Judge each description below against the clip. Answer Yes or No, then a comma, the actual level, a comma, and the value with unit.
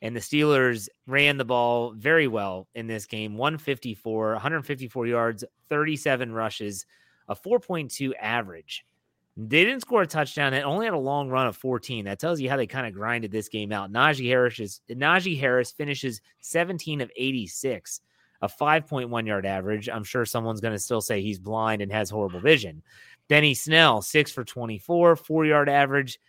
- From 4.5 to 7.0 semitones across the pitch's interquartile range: Yes, average, 4.9 semitones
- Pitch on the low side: Yes, low, 125 Hz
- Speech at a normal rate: Yes, average, 175 wpm